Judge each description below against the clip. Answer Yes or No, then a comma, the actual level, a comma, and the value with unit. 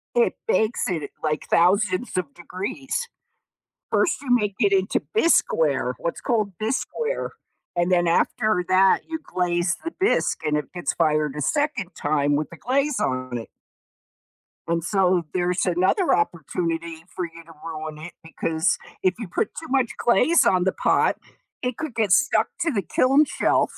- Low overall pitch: No, medium, 185 Hz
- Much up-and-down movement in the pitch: Yes, wide, 7.3 semitones